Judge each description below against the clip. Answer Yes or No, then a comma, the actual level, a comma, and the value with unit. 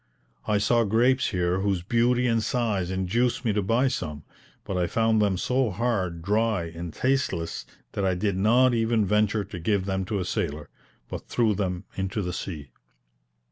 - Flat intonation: No, average, 4.0 semitones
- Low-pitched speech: Yes, low, 100 Hz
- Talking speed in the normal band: Yes, average, 180 wpm